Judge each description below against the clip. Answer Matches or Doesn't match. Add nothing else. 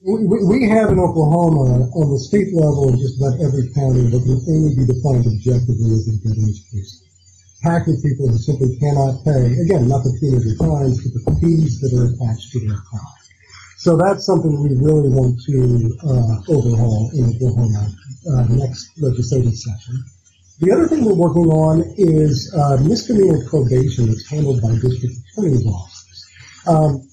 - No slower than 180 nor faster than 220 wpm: Doesn't match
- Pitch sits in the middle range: Doesn't match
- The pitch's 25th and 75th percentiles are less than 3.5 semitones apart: Doesn't match